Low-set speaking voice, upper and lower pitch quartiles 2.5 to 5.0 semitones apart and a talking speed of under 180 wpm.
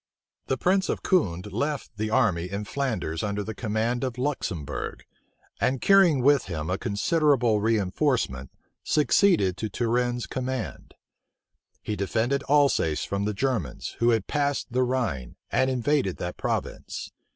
No: low, 120 Hz; wide, 5.5 semitones; average, 140 wpm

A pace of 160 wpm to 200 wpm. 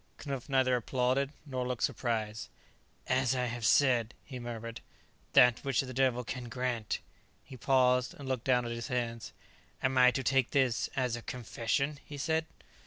Yes: average, 175 wpm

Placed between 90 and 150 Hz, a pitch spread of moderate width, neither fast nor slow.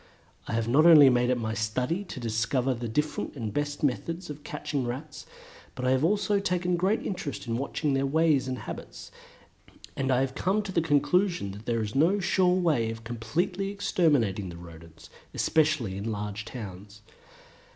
No: low, 135 Hz; wide, 6.8 semitones; average, 180 wpm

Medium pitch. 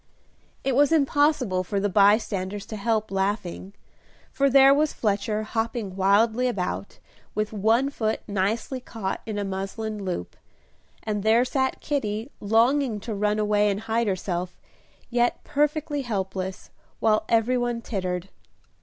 No: high, 215 Hz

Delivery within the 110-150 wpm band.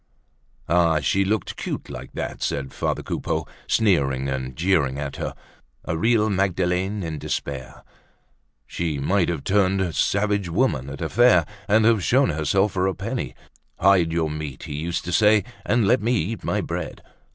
No: average, 165 wpm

